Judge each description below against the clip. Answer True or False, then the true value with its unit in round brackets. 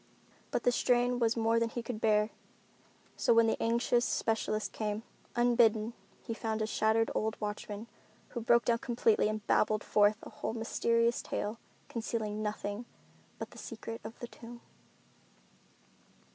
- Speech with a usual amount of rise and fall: False (1.5 semitones)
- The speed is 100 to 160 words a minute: True (150 wpm)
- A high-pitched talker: True (225 Hz)